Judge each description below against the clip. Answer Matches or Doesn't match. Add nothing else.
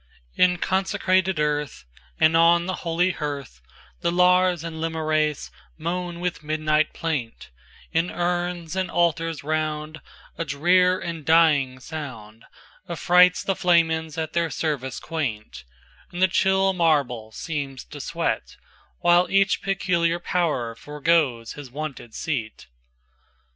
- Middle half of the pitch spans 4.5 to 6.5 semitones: Doesn't match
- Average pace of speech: Doesn't match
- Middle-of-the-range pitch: Matches